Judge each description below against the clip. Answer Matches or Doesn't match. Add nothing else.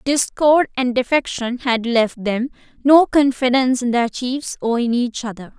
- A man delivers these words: Doesn't match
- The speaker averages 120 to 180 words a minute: Matches